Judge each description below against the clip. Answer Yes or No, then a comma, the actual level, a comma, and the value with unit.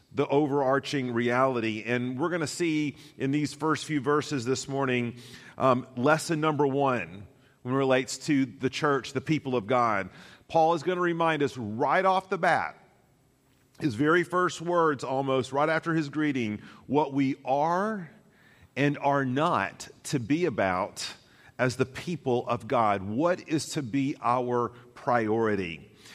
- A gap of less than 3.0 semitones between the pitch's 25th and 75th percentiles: No, average, 3.9 semitones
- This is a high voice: No, medium, 140 Hz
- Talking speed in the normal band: Yes, average, 155 wpm